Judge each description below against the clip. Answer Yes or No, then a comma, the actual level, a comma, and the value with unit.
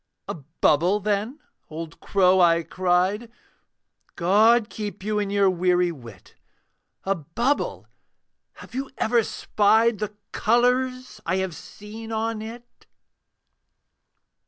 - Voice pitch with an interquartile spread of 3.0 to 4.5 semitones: Yes, average, 3.9 semitones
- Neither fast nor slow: No, slow, 110 wpm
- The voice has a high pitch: Yes, high, 205 Hz